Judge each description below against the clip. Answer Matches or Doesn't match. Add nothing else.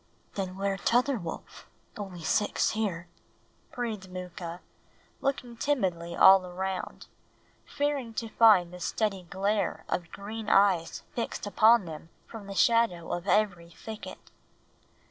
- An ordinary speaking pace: Doesn't match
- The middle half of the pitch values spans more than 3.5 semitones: Matches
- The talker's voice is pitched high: Matches